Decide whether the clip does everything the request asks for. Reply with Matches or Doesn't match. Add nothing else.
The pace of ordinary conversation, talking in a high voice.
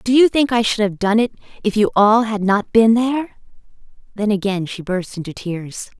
Doesn't match